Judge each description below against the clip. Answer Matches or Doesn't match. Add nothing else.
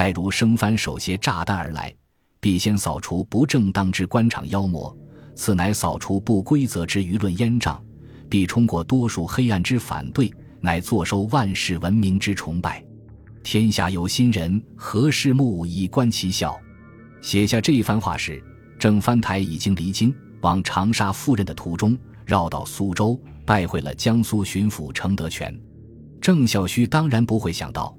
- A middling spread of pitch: Matches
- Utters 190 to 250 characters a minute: Matches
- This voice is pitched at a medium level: Doesn't match